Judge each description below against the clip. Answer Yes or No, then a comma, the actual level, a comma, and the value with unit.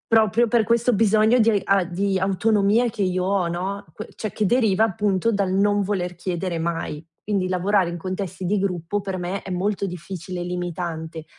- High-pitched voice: Yes, high, 195 Hz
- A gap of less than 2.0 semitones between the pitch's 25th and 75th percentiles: No, average, 2.7 semitones